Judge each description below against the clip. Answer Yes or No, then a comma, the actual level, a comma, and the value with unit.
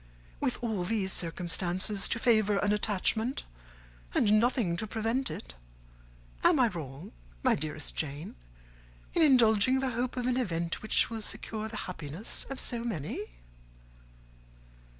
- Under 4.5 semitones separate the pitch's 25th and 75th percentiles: No, average, 5.1 semitones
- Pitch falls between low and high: No, high, 215 Hz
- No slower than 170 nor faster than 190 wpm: No, slow, 135 wpm